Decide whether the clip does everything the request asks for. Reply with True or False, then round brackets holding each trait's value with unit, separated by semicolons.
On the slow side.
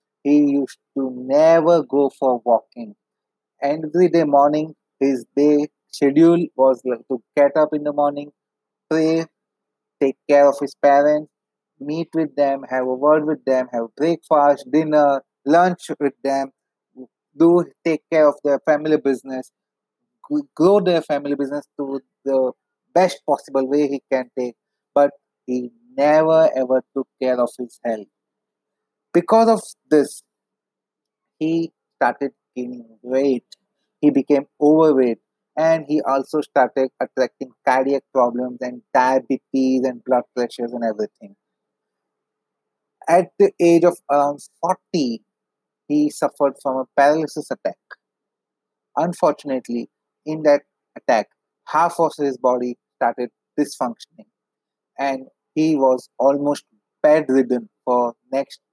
True (125 wpm)